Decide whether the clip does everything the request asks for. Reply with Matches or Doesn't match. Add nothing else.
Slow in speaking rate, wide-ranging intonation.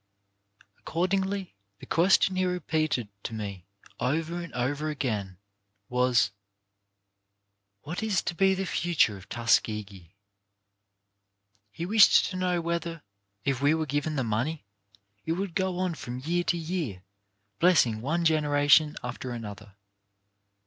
Matches